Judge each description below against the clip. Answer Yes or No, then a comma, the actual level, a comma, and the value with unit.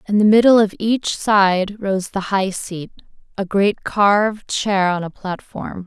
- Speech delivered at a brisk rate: No, average, 175 wpm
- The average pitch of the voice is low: No, high, 200 Hz